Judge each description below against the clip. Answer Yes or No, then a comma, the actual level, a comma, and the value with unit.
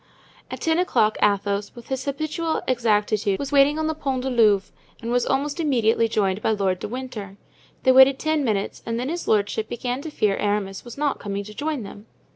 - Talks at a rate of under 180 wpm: No, fast, 205 wpm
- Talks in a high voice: Yes, high, 240 Hz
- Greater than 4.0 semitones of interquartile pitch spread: Yes, average, 5.2 semitones